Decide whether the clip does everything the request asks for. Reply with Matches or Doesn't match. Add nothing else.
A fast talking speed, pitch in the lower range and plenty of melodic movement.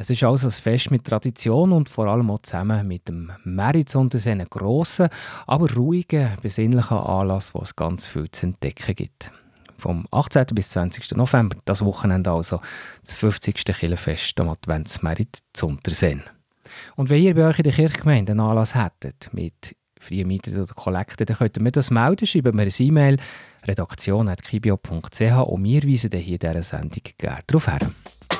Doesn't match